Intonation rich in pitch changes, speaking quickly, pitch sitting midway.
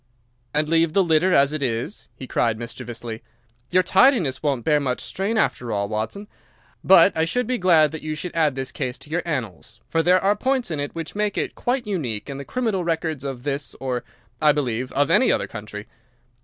Yes: wide, 6.2 semitones; fast, 210 wpm; medium, 150 Hz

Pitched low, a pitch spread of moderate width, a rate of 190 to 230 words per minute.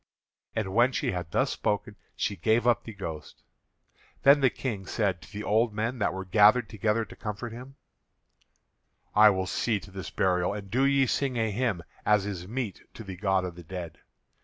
Yes: low, 105 Hz; average, 3.5 semitones; average, 195 wpm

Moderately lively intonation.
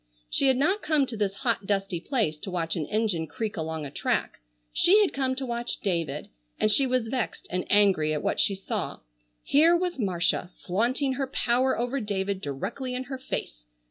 No: wide, 6.5 semitones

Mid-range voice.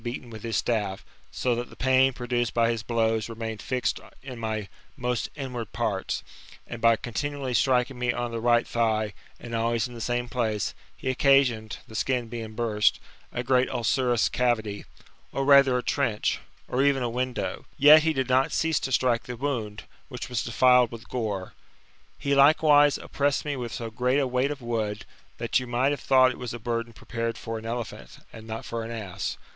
No: low, 120 Hz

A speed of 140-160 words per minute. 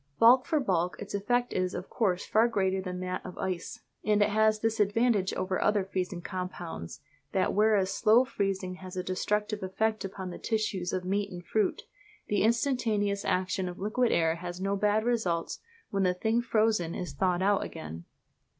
No: average, 180 wpm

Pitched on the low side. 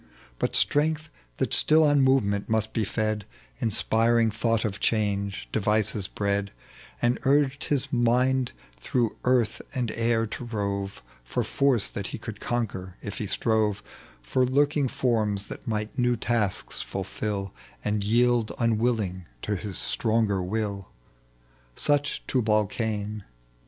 Yes: low, 110 Hz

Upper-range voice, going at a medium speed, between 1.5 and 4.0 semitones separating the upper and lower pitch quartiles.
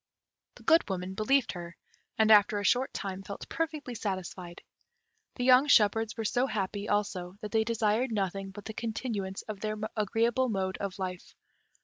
Yes: high, 210 Hz; average, 165 wpm; average, 3.2 semitones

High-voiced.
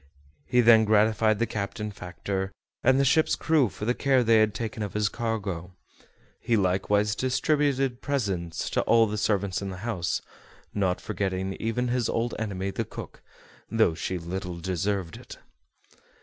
No: low, 105 Hz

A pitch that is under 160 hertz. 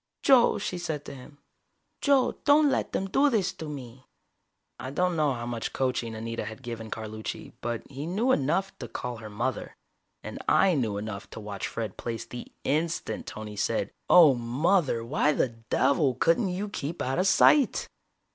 Yes: low, 135 Hz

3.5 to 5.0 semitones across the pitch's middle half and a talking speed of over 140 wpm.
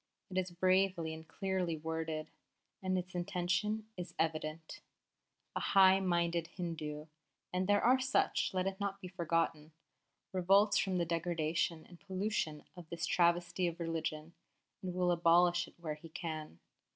No: narrow, 2.5 semitones; average, 150 wpm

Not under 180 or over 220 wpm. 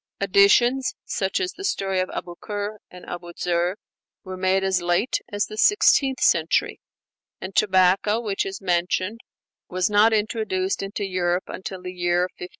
No: average, 155 wpm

